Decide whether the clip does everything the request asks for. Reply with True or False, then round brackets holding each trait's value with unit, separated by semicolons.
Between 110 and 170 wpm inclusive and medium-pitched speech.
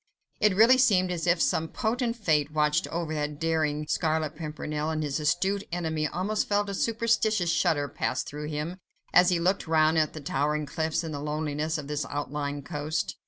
False (185 wpm; 160 Hz)